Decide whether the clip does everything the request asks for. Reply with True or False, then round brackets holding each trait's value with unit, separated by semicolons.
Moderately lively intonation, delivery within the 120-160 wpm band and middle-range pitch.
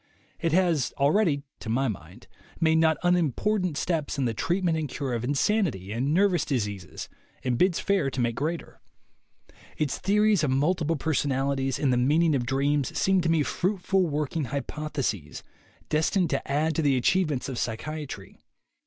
False (4.4 semitones; 170 wpm; 150 Hz)